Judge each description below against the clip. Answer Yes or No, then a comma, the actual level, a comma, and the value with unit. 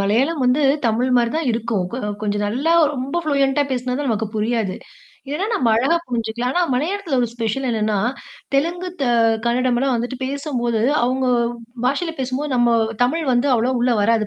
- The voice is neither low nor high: No, very high, 250 Hz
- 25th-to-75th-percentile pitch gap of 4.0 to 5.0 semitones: No, average, 3.3 semitones